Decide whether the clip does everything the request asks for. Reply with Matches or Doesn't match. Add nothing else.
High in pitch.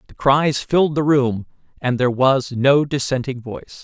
Doesn't match